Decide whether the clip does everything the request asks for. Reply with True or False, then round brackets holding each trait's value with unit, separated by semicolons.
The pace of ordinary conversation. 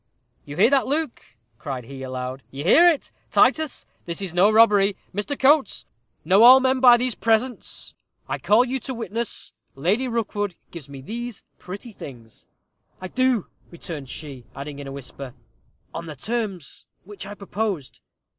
True (160 wpm)